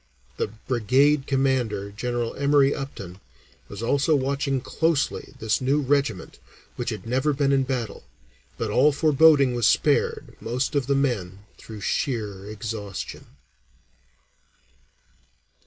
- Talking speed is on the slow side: Yes, slow, 125 wpm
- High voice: No, low, 130 Hz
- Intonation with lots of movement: No, average, 4.2 semitones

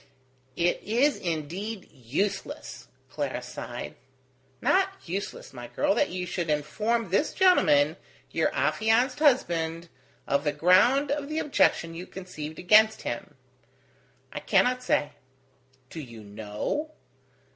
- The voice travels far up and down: Yes, wide, 8.5 semitones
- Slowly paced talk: Yes, slow, 120 wpm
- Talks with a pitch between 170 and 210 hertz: Yes, medium, 185 Hz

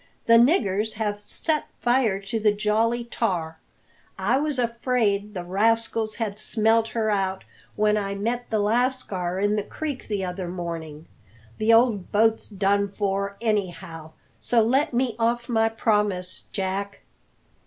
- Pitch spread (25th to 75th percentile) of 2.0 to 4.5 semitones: Yes, average, 2.8 semitones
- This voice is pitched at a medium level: No, high, 210 Hz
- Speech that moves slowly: No, average, 145 wpm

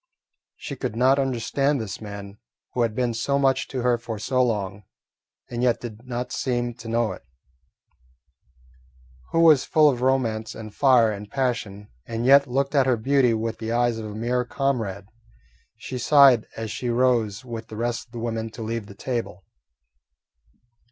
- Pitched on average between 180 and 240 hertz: No, low, 120 Hz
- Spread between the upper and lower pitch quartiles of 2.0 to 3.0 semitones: Yes, narrow, 2.6 semitones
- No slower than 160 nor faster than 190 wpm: Yes, average, 175 wpm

